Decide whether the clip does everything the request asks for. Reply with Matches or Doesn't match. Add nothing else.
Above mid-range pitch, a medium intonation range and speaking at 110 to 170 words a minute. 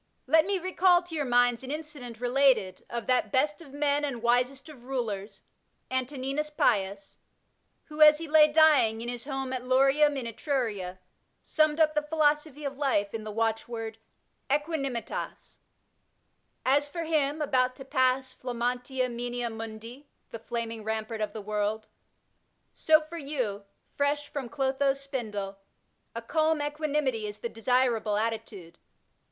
Matches